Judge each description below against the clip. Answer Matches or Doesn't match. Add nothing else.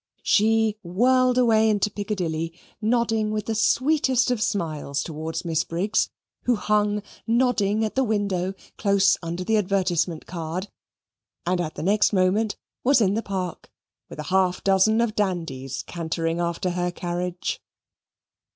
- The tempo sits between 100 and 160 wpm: Matches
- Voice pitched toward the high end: Matches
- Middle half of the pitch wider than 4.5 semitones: Doesn't match